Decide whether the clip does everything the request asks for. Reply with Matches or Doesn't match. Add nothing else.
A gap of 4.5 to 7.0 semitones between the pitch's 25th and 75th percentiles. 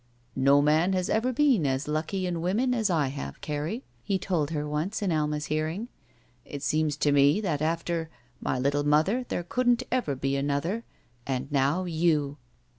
Matches